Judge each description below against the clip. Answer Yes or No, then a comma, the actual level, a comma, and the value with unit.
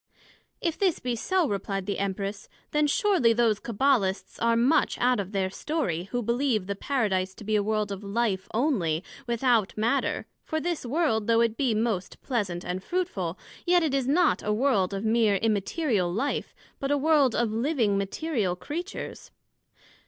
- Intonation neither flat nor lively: No, wide, 5.9 semitones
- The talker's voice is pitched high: Yes, high, 230 Hz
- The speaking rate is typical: Yes, average, 170 wpm